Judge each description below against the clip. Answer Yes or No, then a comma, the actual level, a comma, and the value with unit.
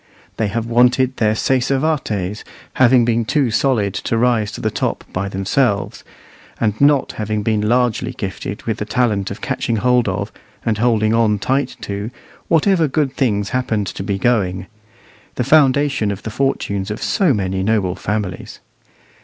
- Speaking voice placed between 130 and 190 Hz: No, low, 110 Hz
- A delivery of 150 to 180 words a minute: Yes, average, 160 wpm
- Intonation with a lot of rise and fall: No, average, 3.9 semitones